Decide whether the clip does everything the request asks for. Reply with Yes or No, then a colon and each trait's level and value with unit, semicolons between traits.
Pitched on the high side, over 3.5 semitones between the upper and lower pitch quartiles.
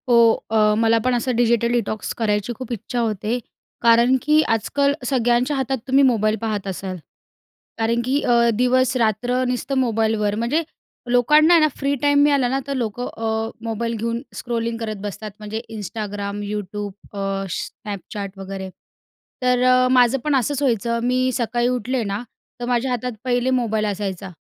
No: high, 235 Hz; average, 2.8 semitones